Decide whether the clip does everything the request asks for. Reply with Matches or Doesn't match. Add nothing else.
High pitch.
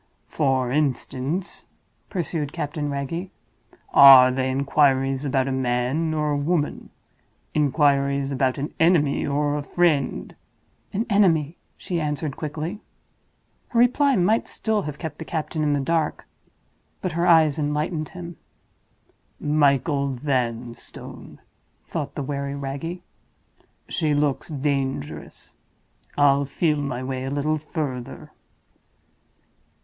Doesn't match